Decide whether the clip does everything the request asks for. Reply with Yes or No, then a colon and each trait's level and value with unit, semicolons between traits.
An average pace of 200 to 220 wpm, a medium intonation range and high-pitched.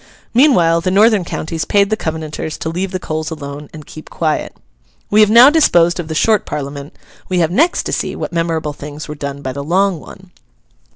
No: fast, 205 wpm; average, 4.3 semitones; medium, 165 Hz